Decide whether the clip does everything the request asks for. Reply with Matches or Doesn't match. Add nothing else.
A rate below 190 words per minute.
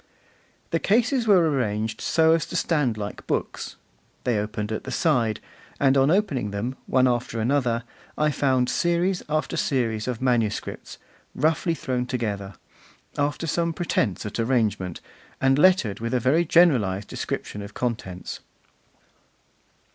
Matches